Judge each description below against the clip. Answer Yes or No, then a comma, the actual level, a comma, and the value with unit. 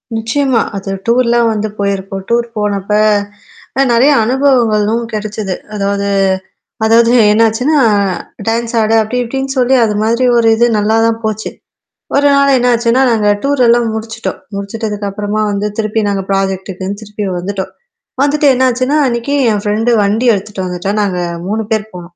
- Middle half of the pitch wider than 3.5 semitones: No, average, 2.8 semitones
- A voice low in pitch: No, high, 220 Hz